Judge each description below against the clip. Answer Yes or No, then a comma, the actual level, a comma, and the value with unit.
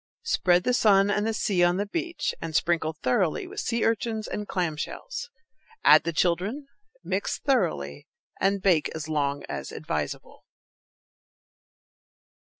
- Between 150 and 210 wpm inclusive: No, average, 140 wpm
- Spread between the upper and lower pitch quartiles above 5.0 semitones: Yes, wide, 5.6 semitones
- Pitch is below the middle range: No, high, 195 Hz